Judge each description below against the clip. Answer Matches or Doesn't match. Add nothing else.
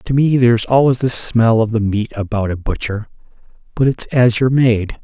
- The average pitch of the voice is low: Matches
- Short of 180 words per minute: Doesn't match